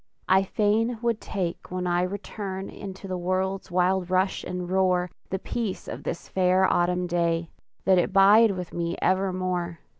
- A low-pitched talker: No, medium, 185 Hz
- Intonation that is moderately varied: No, narrow, 1.4 semitones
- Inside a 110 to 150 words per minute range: No, average, 160 wpm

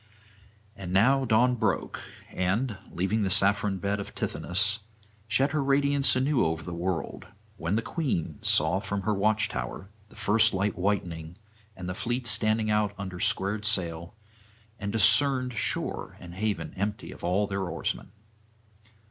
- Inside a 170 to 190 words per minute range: No, average, 150 wpm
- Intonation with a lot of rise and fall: No, average, 3.5 semitones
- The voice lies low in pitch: Yes, low, 100 Hz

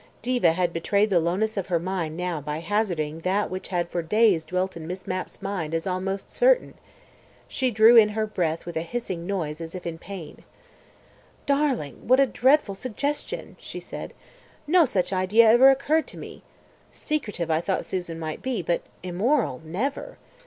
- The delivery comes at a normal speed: Yes, average, 175 wpm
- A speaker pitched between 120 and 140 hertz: No, medium, 185 Hz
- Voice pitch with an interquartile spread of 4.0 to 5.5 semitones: Yes, average, 5.2 semitones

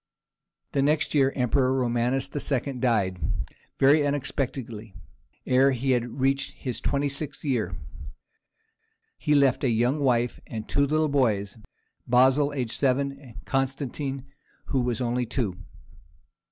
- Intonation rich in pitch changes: No, narrow, 2.6 semitones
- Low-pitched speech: Yes, low, 130 Hz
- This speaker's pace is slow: Yes, slow, 130 wpm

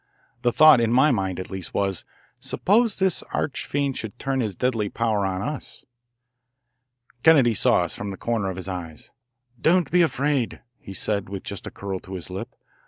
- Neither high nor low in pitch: No, low, 115 Hz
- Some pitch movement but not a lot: No, wide, 6.3 semitones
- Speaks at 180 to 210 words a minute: Yes, average, 185 wpm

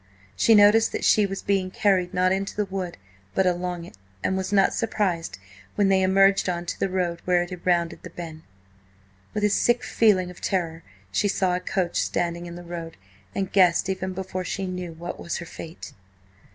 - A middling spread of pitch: No, narrow, 2.0 semitones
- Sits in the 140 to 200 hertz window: Yes, medium, 185 Hz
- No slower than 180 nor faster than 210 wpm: Yes, average, 200 wpm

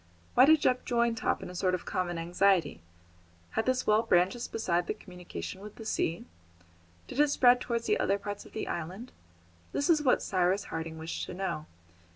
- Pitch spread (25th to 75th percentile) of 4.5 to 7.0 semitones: Yes, average, 5.1 semitones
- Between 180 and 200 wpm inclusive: Yes, average, 190 wpm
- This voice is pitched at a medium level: No, high, 195 Hz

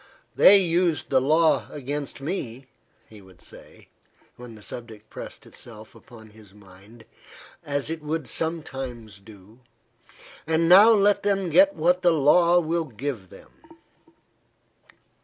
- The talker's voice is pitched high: No, medium, 140 Hz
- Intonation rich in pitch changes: Yes, wide, 7.2 semitones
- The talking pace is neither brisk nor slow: No, slow, 130 wpm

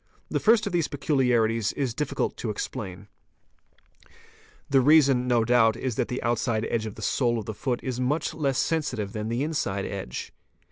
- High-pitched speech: No, low, 125 Hz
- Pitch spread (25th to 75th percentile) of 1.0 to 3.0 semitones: No, average, 3.8 semitones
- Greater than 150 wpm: Yes, average, 180 wpm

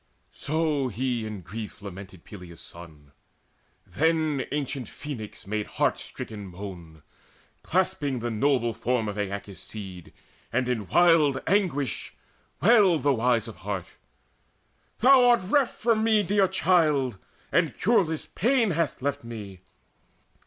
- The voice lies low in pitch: Yes, low, 130 Hz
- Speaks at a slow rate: Yes, slow, 130 wpm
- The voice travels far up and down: Yes, wide, 8.2 semitones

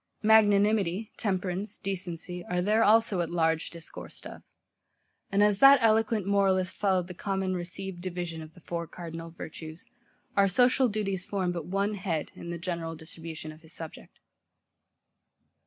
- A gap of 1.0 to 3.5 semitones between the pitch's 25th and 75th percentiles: Yes, average, 3.1 semitones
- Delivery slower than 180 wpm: Yes, average, 150 wpm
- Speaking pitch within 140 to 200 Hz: Yes, medium, 185 Hz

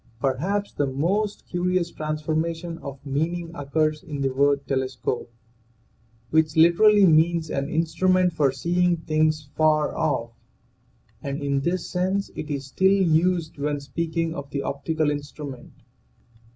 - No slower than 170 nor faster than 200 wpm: No, slow, 135 wpm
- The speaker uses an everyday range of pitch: Yes, average, 3.3 semitones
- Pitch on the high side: No, medium, 155 Hz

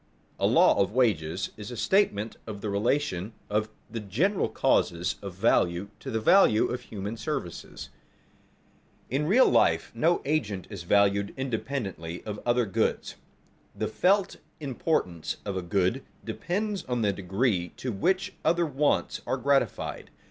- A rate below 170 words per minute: Yes, average, 150 wpm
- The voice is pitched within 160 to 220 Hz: No, low, 110 Hz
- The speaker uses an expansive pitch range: Yes, wide, 6.1 semitones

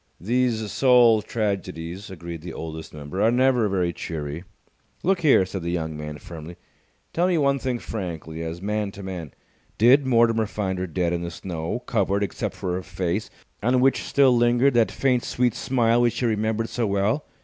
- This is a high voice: No, low, 105 Hz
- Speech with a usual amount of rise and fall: No, wide, 5.8 semitones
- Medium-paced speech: Yes, average, 180 wpm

